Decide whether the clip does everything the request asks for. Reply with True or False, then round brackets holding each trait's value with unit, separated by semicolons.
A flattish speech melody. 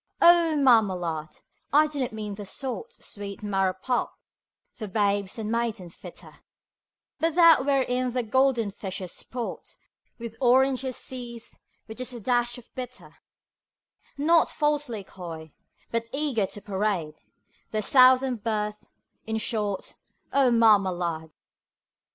False (4.4 semitones)